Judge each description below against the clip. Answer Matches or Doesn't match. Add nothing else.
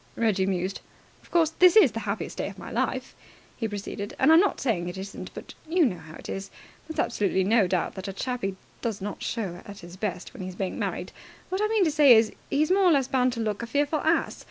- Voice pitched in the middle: Doesn't match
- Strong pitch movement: Matches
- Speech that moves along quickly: Matches